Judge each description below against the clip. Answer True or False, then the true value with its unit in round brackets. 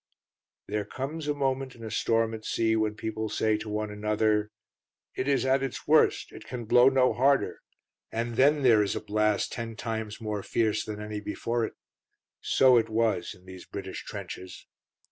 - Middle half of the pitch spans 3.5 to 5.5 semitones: False (3.0 semitones)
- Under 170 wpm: False (185 wpm)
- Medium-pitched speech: False (110 Hz)